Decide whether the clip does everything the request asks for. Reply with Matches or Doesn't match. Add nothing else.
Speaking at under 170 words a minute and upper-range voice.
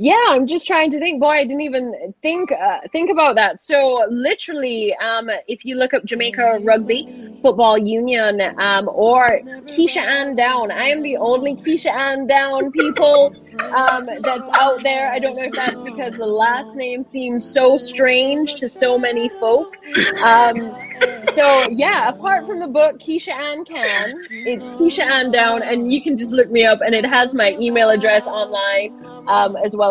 Doesn't match